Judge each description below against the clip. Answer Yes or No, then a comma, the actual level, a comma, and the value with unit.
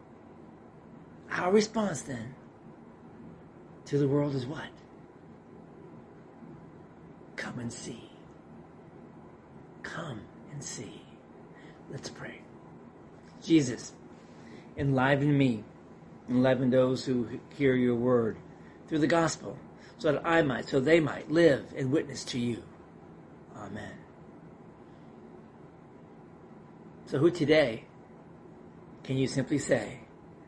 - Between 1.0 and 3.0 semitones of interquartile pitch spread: No, average, 4.4 semitones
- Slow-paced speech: Yes, slow, 95 wpm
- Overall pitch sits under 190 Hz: Yes, low, 135 Hz